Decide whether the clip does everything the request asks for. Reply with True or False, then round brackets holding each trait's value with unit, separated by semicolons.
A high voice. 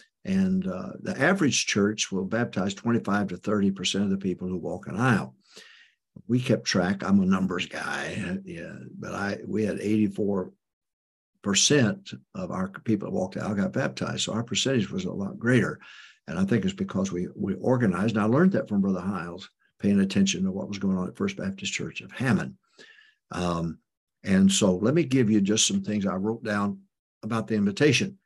False (110 Hz)